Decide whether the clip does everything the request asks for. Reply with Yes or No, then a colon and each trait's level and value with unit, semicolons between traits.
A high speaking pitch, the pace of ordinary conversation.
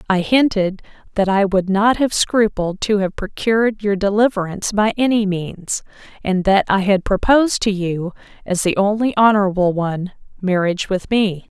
Yes: high, 200 Hz; average, 160 wpm